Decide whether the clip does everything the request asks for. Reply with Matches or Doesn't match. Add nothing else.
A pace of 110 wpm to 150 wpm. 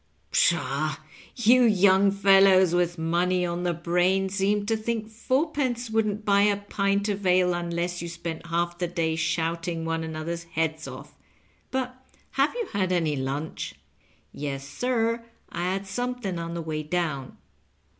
Doesn't match